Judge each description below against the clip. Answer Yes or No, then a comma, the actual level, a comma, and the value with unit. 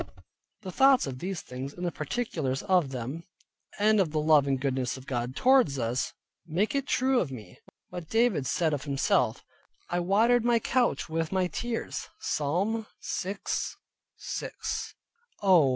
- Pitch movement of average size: No, wide, 7.9 semitones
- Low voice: No, medium, 170 Hz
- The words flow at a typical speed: Yes, average, 150 wpm